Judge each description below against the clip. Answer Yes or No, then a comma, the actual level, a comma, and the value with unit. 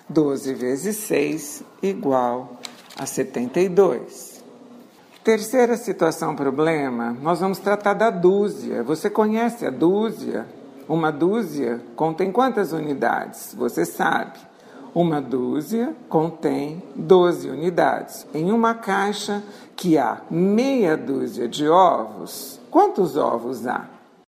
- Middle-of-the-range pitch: Yes, medium, 175 Hz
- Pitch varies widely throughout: Yes, wide, 5.8 semitones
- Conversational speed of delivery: No, slow, 105 wpm